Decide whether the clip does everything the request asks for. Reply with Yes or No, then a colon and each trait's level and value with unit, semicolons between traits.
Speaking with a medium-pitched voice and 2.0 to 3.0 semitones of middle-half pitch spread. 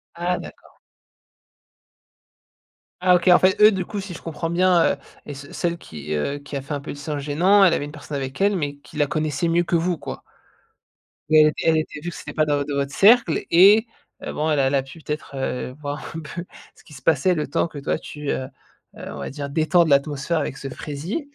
No: medium, 155 Hz; average, 3.4 semitones